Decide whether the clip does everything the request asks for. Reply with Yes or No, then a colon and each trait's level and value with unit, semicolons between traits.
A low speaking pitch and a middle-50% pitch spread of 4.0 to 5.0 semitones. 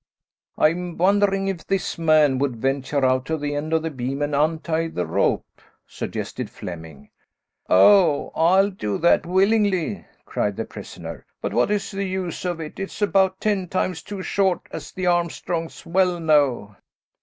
No: medium, 165 Hz; average, 4.7 semitones